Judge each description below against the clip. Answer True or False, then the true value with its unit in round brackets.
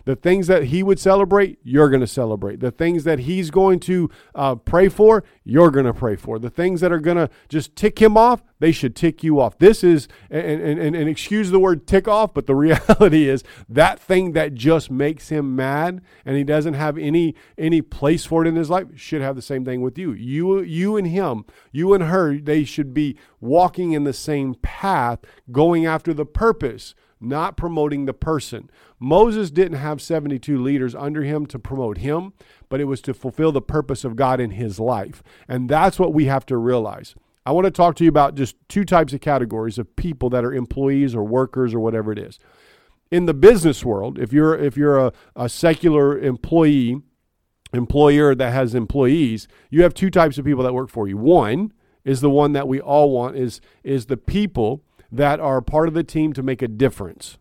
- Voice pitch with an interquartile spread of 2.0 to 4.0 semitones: False (4.5 semitones)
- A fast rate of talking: True (210 wpm)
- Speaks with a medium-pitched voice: True (145 Hz)